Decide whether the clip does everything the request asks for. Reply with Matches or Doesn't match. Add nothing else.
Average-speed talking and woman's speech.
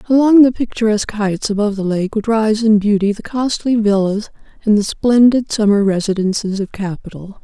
Matches